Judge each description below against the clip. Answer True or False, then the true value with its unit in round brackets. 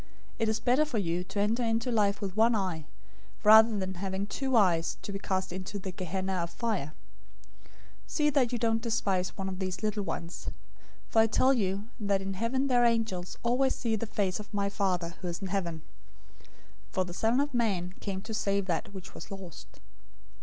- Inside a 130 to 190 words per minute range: False (205 wpm)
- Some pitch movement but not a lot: True (3.4 semitones)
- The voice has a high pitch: True (200 Hz)